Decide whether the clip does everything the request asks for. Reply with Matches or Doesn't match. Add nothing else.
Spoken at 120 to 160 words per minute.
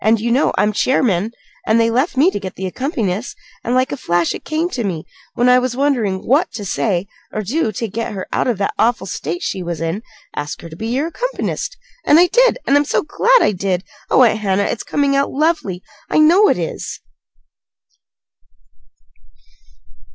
Doesn't match